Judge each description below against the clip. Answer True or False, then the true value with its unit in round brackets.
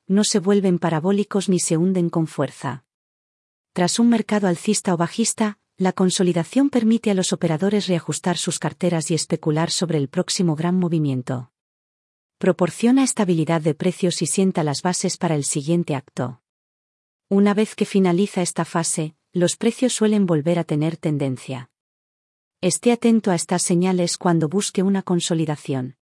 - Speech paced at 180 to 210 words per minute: False (150 wpm)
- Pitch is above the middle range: False (175 Hz)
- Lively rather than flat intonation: False (3.8 semitones)